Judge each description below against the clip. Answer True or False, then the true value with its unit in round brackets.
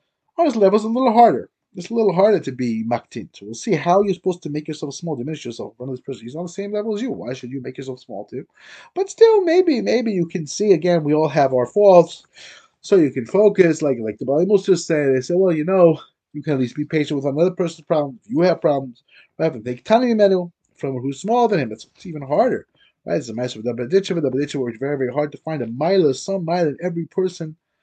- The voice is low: False (165 Hz)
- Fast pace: True (255 wpm)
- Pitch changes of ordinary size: False (6.0 semitones)